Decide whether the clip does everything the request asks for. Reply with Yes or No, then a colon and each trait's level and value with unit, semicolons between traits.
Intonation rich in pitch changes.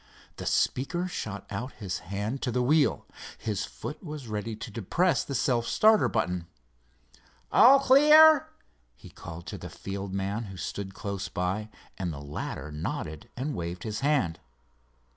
Yes: wide, 7.3 semitones